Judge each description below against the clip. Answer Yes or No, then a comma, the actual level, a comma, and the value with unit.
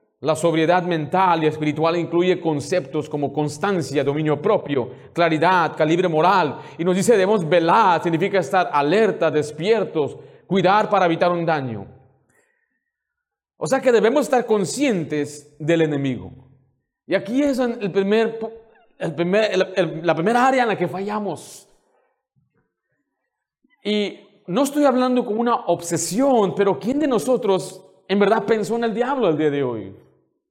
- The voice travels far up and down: Yes, wide, 6.1 semitones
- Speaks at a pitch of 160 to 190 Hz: Yes, medium, 185 Hz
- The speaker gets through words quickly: No, average, 145 wpm